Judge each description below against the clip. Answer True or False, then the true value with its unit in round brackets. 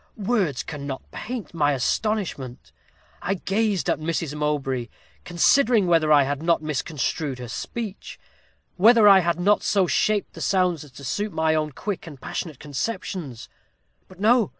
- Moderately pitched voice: True (170 Hz)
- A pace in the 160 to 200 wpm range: False (150 wpm)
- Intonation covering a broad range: True (5.8 semitones)